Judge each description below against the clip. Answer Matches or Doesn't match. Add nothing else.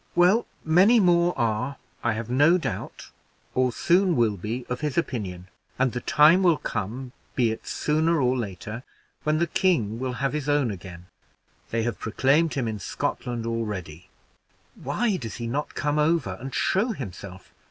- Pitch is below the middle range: Matches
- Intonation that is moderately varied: Doesn't match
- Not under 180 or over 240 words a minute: Doesn't match